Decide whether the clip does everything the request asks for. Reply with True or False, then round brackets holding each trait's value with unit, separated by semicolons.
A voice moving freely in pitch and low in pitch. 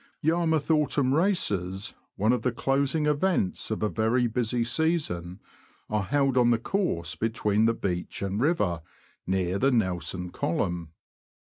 True (7.0 semitones; 115 Hz)